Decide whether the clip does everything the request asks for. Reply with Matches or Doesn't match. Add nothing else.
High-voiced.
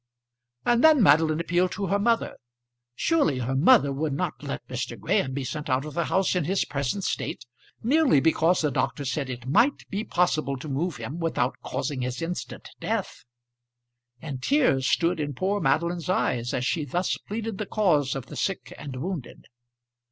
Doesn't match